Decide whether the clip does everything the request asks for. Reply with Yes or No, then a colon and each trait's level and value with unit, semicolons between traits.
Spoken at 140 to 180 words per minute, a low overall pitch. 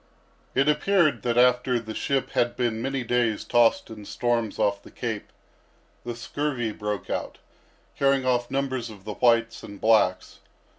Yes: average, 155 wpm; low, 120 Hz